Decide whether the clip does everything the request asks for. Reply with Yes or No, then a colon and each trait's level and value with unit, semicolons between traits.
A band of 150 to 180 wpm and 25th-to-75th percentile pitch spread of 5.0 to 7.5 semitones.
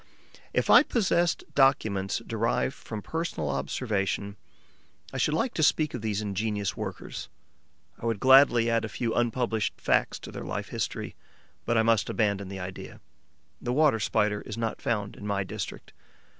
No: average, 160 wpm; average, 3.7 semitones